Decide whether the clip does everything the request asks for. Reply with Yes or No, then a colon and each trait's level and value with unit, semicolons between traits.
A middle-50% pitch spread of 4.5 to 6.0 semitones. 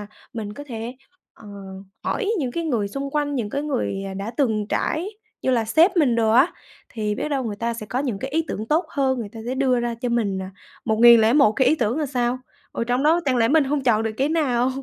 No: average, 4.1 semitones